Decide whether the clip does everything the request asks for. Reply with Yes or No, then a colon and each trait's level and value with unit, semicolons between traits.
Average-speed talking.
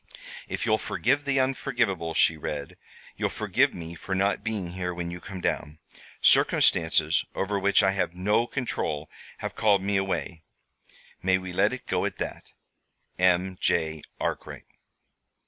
Yes: average, 150 wpm